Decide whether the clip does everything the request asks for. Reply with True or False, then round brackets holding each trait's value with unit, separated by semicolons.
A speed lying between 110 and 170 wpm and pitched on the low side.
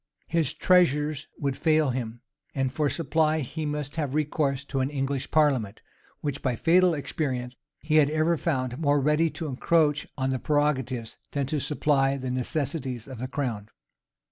False (165 wpm; 145 Hz)